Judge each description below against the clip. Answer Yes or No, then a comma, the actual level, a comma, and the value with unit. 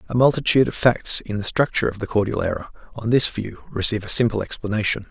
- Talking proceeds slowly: No, average, 200 wpm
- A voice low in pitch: Yes, low, 110 Hz